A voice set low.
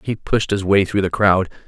Yes: very low, 95 Hz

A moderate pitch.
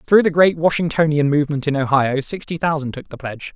Yes: medium, 150 Hz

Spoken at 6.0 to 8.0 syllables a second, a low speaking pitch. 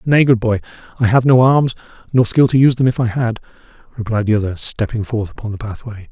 Yes: 6.2 syllables/s; low, 115 Hz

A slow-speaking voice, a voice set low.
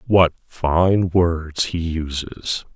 Yes: slow, 110 wpm; very low, 85 Hz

